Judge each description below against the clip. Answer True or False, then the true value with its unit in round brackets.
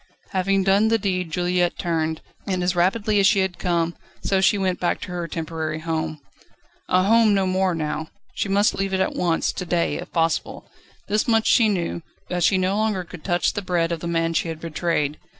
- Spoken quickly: True (210 wpm)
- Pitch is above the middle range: False (180 Hz)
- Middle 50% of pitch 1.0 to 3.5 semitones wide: True (2.7 semitones)